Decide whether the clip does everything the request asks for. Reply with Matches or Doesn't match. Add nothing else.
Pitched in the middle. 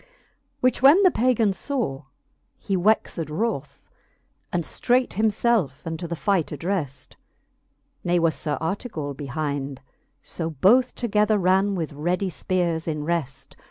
Matches